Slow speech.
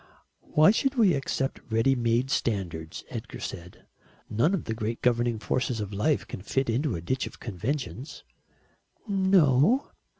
No: average, 145 wpm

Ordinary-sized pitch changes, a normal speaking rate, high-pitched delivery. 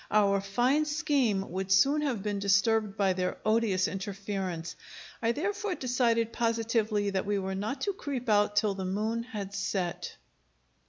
Yes: average, 3.5 semitones; average, 155 wpm; high, 210 Hz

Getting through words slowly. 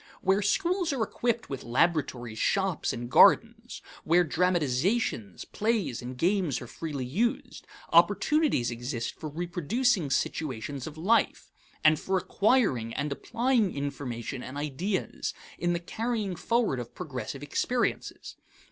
Yes: slow, 125 wpm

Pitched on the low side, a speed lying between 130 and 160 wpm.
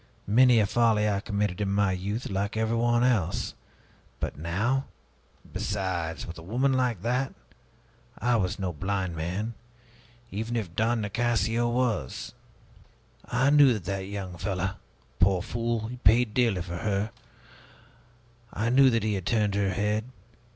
Yes: low, 105 Hz; average, 145 wpm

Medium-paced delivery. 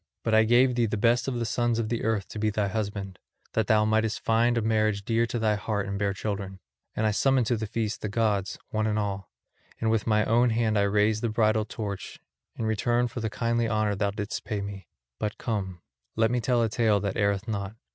No: fast, 230 wpm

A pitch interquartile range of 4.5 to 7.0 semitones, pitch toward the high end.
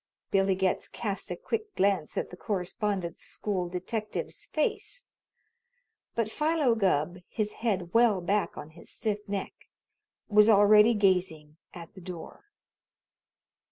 No: average, 3.5 semitones; high, 200 Hz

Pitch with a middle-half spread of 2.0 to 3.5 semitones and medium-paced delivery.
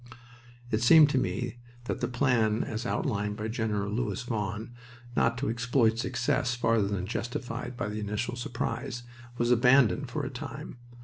Yes: narrow, 2.5 semitones; average, 160 wpm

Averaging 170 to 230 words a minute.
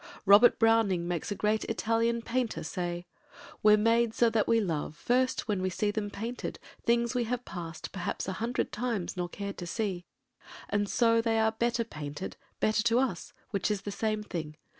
Yes: average, 180 wpm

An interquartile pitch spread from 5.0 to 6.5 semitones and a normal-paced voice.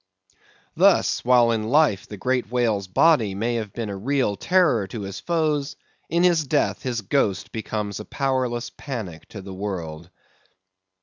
Yes: wide, 5.4 semitones; average, 160 wpm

